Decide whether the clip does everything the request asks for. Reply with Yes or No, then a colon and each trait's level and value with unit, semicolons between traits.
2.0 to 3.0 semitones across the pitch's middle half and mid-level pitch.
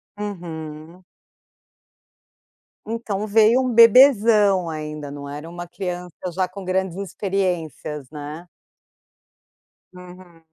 No: average, 4.2 semitones; medium, 180 Hz